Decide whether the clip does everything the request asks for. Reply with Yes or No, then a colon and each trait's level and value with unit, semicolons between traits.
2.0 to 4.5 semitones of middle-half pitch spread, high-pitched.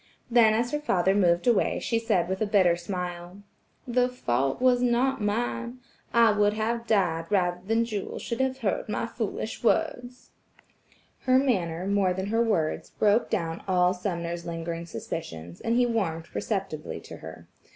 No: average, 5.0 semitones; high, 205 Hz